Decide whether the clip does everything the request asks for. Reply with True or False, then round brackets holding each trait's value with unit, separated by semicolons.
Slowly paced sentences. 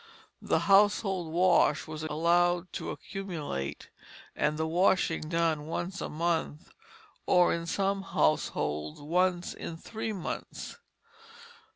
True (110 wpm)